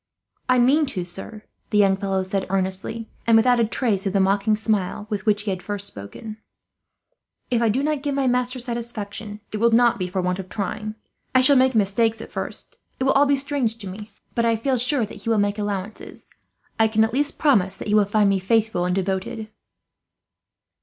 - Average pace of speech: No, fast, 215 wpm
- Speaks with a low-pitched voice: No, high, 215 Hz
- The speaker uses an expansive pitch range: No, average, 3.4 semitones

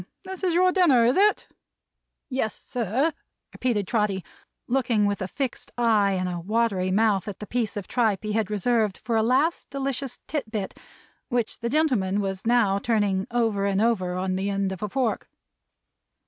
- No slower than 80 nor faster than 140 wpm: No, average, 175 wpm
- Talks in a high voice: Yes, high, 220 Hz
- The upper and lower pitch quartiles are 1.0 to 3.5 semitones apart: No, average, 4.0 semitones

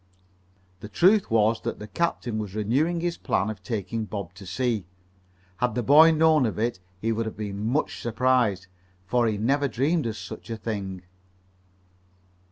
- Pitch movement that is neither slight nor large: Yes, average, 4.2 semitones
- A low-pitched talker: Yes, low, 115 Hz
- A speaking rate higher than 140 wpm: Yes, average, 170 wpm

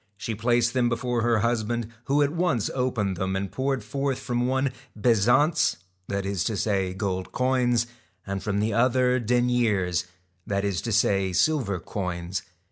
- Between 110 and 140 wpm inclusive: No, average, 160 wpm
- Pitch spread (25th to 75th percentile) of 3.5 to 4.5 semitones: Yes, average, 4.2 semitones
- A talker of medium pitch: No, low, 115 Hz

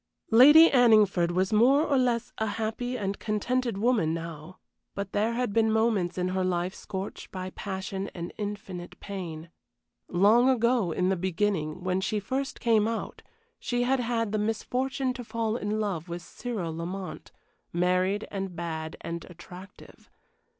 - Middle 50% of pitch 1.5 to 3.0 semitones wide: No, average, 4.3 semitones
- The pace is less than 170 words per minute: Yes, average, 155 wpm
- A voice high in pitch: Yes, high, 200 Hz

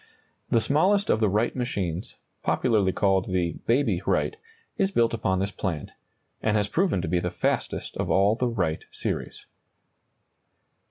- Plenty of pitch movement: No, average, 4.4 semitones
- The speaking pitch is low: Yes, low, 105 Hz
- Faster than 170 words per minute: No, average, 160 wpm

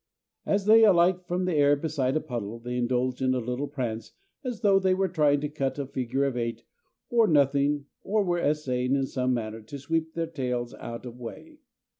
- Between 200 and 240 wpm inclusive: Yes, fast, 205 wpm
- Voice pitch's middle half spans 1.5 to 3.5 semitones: No, wide, 5.5 semitones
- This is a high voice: No, medium, 140 Hz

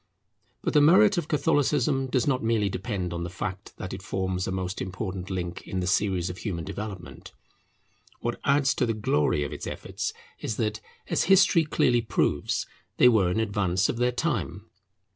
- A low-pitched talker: Yes, low, 105 Hz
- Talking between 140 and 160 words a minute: No, average, 180 wpm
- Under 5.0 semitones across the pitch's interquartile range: No, average, 5.3 semitones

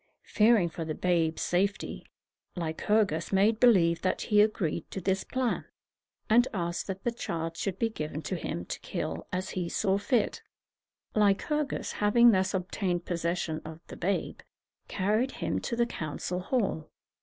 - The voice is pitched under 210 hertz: Yes, high, 190 Hz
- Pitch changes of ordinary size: Yes, average, 4.2 semitones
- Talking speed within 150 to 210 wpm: Yes, average, 155 wpm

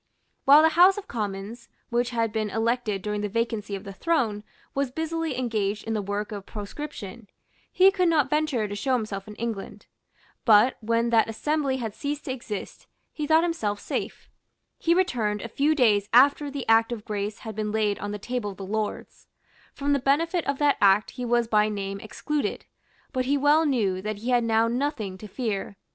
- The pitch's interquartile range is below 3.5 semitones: No, average, 5.1 semitones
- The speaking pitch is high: Yes, high, 230 Hz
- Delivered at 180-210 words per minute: Yes, average, 195 wpm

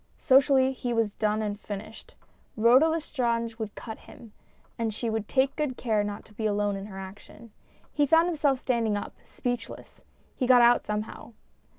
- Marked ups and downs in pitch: No, average, 3.5 semitones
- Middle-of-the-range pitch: No, high, 230 Hz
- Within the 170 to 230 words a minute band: Yes, average, 175 wpm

